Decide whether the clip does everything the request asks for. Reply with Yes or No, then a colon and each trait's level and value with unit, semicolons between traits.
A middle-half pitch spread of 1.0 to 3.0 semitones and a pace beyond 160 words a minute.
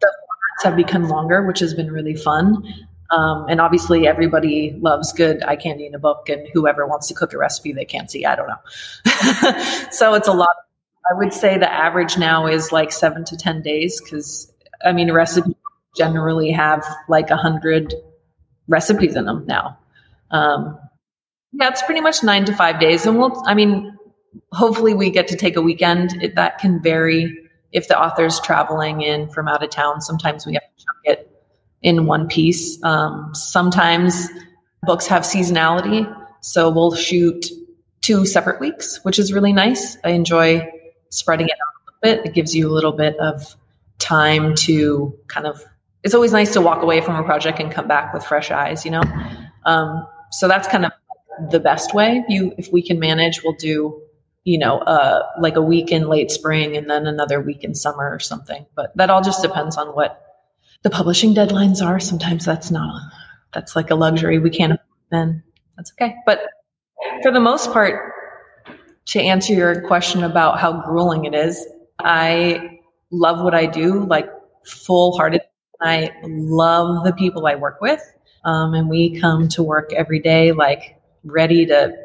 Yes: average, 2.7 semitones; average, 180 wpm